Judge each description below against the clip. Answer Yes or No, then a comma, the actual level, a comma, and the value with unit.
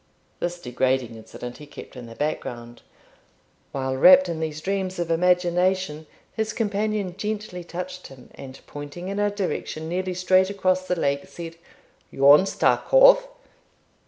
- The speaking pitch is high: No, medium, 175 Hz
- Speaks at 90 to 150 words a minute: Yes, average, 145 wpm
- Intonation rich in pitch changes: No, average, 4.8 semitones